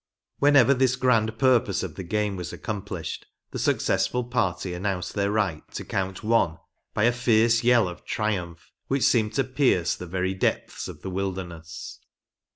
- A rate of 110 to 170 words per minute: Yes, average, 165 wpm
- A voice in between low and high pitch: No, low, 105 Hz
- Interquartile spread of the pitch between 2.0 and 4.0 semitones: No, average, 4.7 semitones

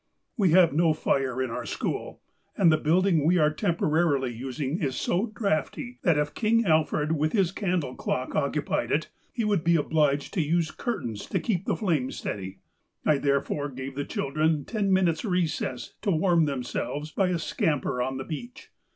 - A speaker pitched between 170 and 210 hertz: No, medium, 155 Hz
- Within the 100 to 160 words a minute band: No, average, 180 wpm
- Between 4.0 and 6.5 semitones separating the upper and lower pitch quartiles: Yes, average, 4.5 semitones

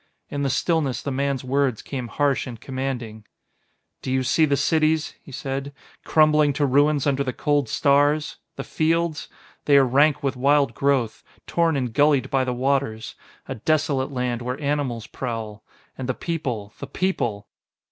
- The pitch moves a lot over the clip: No, narrow, 2.6 semitones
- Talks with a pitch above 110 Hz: Yes, medium, 140 Hz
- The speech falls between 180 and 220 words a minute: No, average, 165 wpm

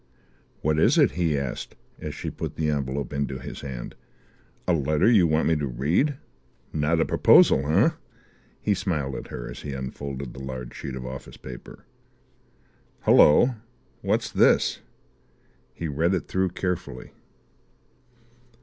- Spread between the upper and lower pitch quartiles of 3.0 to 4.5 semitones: Yes, average, 4.0 semitones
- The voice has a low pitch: Yes, very low, 75 Hz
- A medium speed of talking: Yes, average, 145 wpm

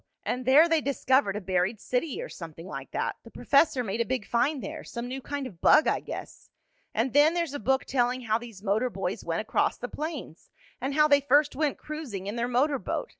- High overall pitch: Yes, very high, 255 Hz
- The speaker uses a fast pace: Yes, fast, 225 wpm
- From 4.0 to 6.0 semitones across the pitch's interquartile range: Yes, average, 4.4 semitones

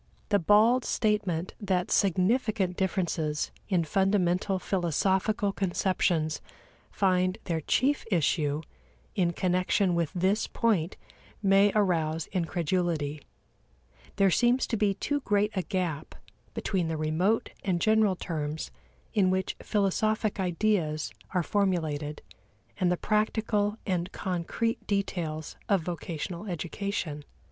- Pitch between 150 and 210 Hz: Yes, medium, 185 Hz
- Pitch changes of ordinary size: Yes, average, 3.4 semitones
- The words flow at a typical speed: No, slow, 110 wpm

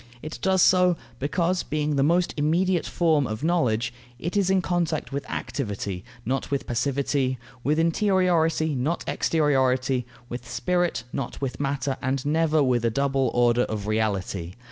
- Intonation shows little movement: No, average, 5.1 semitones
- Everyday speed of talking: Yes, average, 150 wpm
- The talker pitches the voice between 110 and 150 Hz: Yes, medium, 140 Hz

